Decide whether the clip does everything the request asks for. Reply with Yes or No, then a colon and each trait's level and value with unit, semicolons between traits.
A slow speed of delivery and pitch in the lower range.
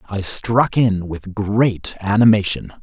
Yes: slow, 125 wpm; low, 105 Hz